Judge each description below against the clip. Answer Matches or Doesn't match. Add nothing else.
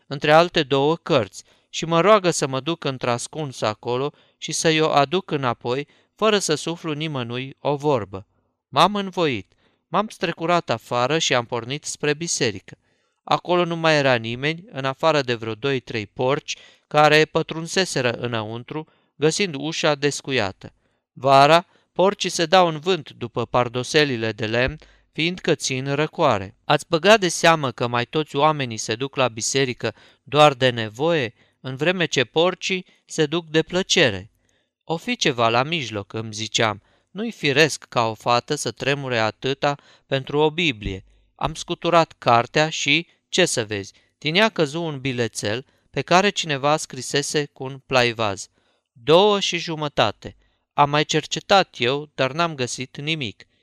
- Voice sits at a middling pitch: Matches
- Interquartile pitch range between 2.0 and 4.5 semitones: Doesn't match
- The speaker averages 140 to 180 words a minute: Matches